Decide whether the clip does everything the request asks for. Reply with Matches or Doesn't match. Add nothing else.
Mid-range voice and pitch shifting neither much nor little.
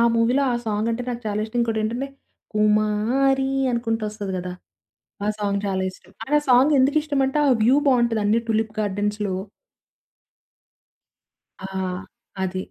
Doesn't match